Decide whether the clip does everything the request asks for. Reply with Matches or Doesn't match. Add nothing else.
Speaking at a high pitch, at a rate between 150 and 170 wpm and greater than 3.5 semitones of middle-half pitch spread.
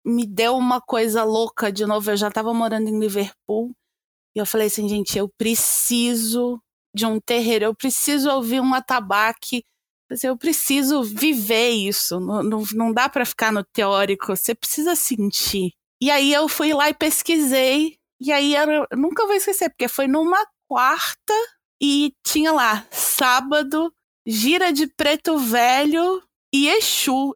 Matches